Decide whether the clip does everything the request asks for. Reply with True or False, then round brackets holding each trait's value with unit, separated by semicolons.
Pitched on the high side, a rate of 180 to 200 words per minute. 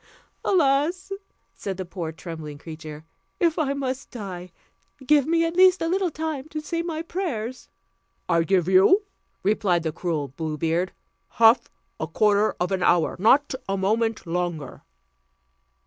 False (210 Hz; 145 wpm)